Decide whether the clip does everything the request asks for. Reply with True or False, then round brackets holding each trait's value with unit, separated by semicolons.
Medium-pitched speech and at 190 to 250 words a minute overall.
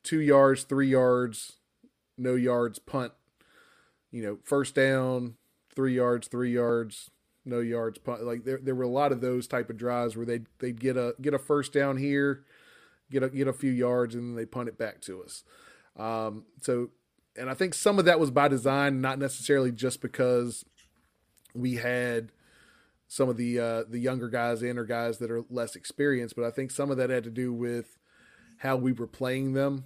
False (125 Hz; 200 wpm)